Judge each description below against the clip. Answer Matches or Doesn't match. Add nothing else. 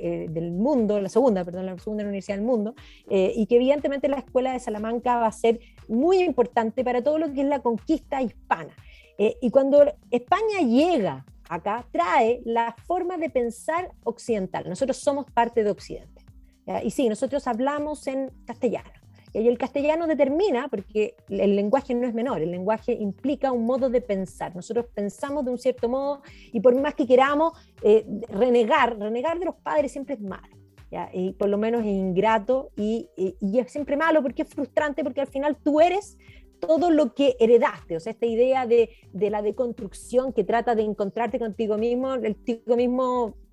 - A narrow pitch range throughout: Doesn't match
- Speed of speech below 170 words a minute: Doesn't match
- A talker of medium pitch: Doesn't match